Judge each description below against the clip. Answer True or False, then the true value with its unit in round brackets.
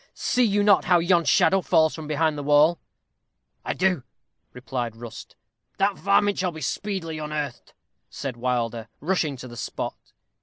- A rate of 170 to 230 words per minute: False (155 wpm)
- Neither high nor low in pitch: True (155 Hz)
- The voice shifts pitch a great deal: True (6.2 semitones)